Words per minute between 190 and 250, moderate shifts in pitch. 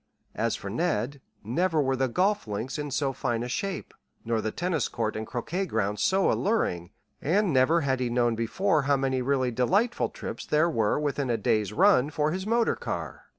No: average, 195 wpm; wide, 6.8 semitones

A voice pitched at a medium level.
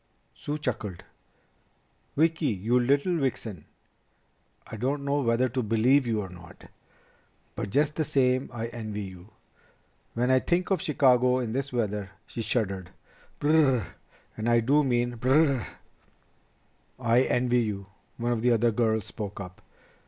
No: low, 120 Hz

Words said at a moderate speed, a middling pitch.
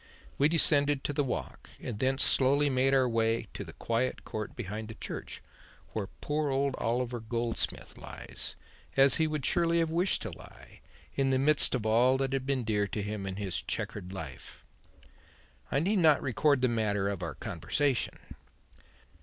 No: average, 175 wpm; low, 130 Hz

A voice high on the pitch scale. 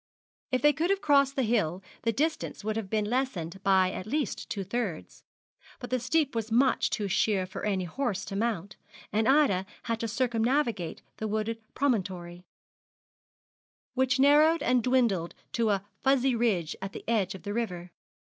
Yes: high, 225 Hz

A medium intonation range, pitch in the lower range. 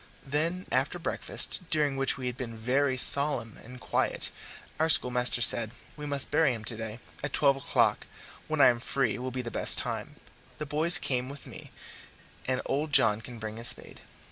Yes: average, 3.3 semitones; low, 130 Hz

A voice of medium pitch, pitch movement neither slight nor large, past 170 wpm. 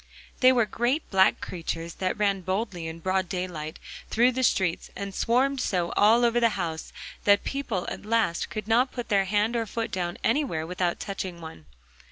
No: high, 200 Hz; average, 4.7 semitones; average, 185 wpm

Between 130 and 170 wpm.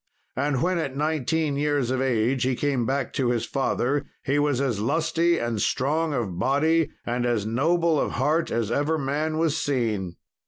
No: average, 180 wpm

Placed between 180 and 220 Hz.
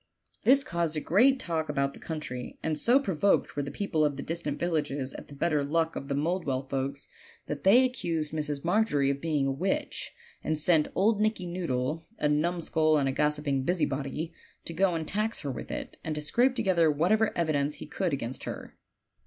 No: medium, 155 Hz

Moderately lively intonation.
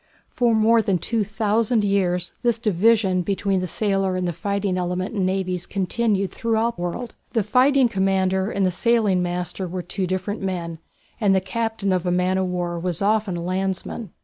Yes: average, 3.1 semitones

